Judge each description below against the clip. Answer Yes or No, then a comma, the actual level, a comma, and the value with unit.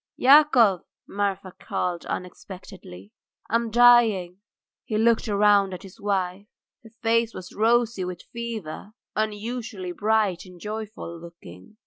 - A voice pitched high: Yes, high, 205 Hz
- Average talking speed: No, slow, 120 wpm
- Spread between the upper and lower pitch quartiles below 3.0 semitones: No, average, 3.8 semitones